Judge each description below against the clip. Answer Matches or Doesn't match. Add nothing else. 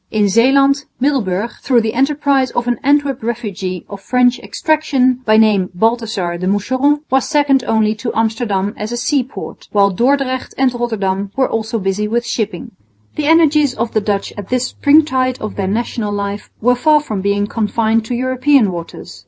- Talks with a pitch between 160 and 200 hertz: Doesn't match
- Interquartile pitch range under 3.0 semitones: Doesn't match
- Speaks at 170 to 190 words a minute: Matches